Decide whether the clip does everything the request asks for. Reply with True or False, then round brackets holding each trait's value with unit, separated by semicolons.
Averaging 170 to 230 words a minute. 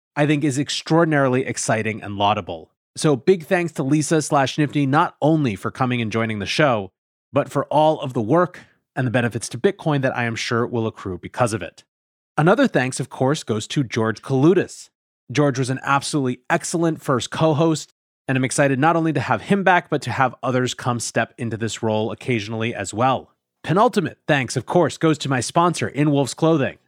True (200 wpm)